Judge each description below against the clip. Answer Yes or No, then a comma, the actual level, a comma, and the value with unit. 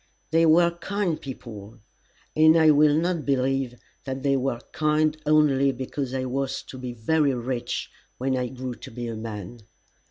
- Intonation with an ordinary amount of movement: Yes, average, 3.6 semitones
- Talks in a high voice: No, low, 135 Hz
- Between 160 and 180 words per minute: Yes, average, 165 wpm